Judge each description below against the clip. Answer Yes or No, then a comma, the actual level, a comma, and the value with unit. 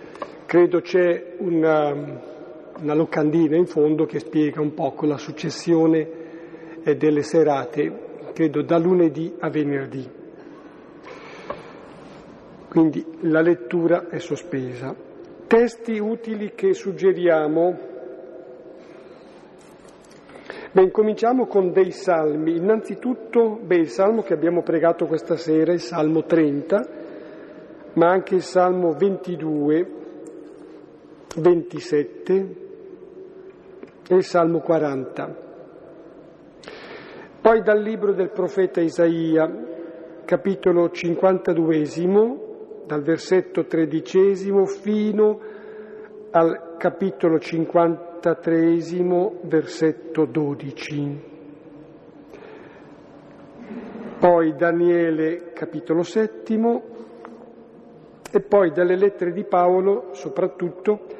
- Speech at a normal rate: No, slow, 80 wpm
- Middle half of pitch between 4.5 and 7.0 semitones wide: No, average, 3.5 semitones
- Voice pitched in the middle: Yes, medium, 170 Hz